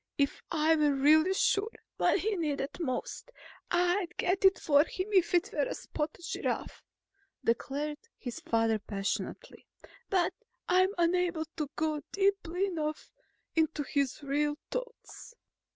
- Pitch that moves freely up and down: No, average, 4.2 semitones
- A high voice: Yes, very high, 320 Hz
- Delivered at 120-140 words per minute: Yes, slow, 135 wpm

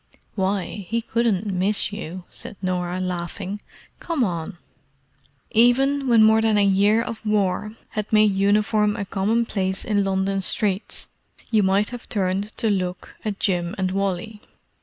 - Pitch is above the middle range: Yes, high, 205 Hz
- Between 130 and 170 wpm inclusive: Yes, average, 145 wpm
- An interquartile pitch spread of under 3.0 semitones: Yes, narrow, 2.4 semitones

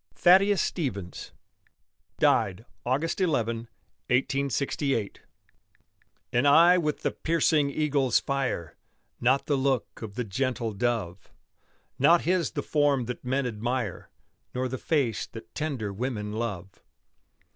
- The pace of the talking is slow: Yes, slow, 115 wpm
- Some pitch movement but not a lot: Yes, average, 4.5 semitones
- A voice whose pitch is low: Yes, low, 130 Hz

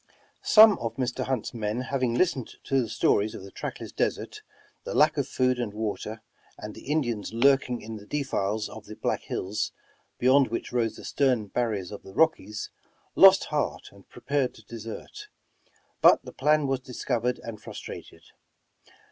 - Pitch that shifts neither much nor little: Yes, average, 3.9 semitones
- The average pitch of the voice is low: Yes, low, 120 Hz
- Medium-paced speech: Yes, average, 165 wpm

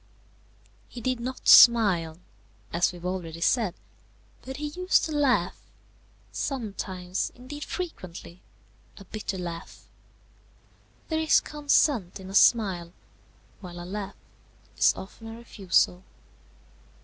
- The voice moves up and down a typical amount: No, wide, 6.4 semitones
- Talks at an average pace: No, slow, 115 wpm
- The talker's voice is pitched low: No, high, 200 Hz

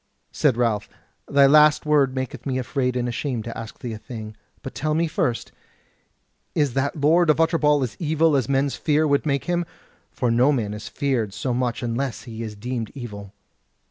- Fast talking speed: No, average, 190 wpm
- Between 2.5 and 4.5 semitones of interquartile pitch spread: Yes, average, 4.2 semitones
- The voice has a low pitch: Yes, low, 130 Hz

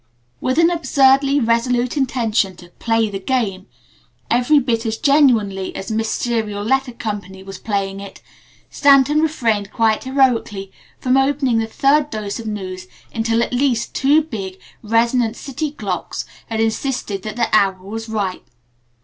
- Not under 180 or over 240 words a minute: No, average, 150 wpm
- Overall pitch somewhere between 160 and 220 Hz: No, high, 230 Hz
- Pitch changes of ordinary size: Yes, average, 4.4 semitones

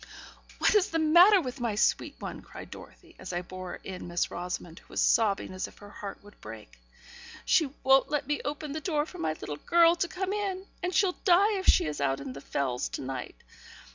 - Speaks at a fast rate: Yes, fast, 220 wpm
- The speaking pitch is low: No, very high, 255 Hz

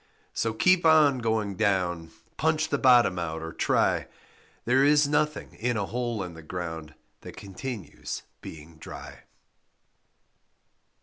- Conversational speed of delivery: No, slow, 130 wpm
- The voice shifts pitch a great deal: Yes, wide, 7.6 semitones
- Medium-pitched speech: No, low, 110 Hz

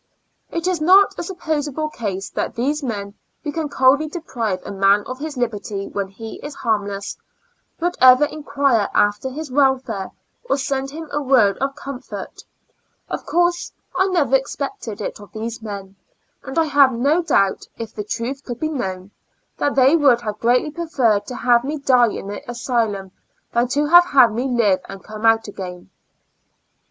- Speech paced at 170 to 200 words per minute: Yes, average, 175 wpm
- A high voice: Yes, very high, 255 Hz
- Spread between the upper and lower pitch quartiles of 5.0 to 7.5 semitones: Yes, wide, 5.6 semitones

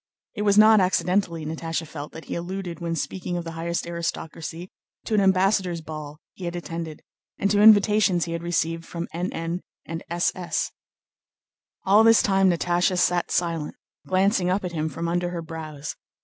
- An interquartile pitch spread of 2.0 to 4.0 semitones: Yes, narrow, 2.4 semitones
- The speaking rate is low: No, average, 170 wpm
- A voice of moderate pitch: Yes, medium, 175 Hz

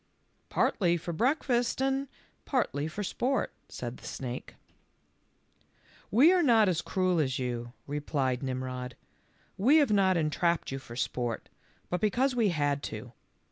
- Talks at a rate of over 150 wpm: No, average, 145 wpm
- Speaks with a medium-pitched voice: Yes, medium, 170 Hz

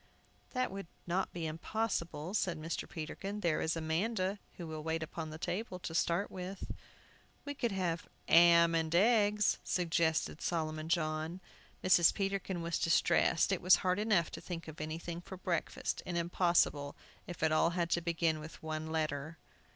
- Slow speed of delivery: No, average, 165 wpm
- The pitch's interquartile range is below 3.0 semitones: Yes, narrow, 2.6 semitones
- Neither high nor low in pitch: Yes, medium, 170 Hz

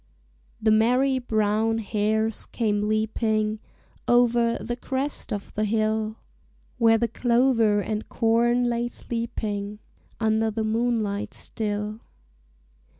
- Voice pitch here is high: Yes, high, 220 Hz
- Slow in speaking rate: Yes, slow, 105 wpm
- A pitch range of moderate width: No, narrow, 1.7 semitones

